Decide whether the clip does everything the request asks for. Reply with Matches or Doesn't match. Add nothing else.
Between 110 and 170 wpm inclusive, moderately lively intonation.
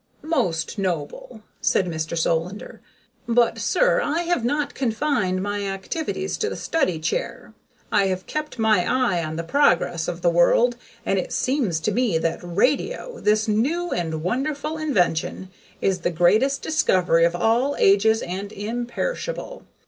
Doesn't match